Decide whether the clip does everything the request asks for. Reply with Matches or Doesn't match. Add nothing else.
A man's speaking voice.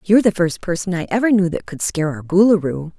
Doesn't match